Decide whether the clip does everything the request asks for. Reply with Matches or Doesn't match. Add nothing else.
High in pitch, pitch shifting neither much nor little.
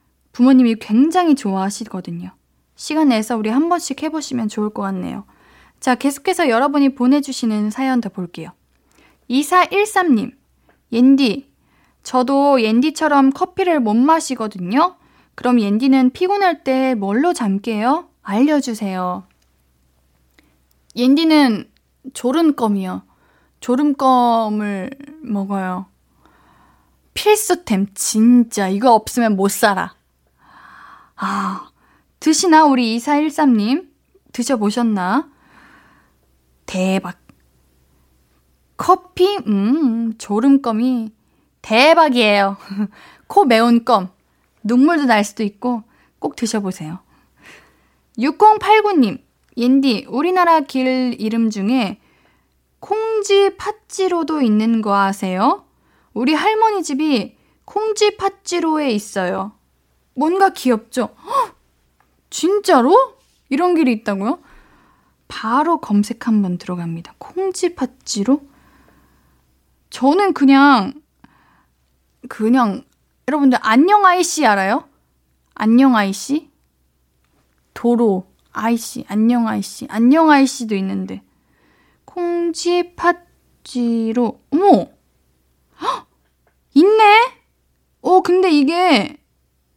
Doesn't match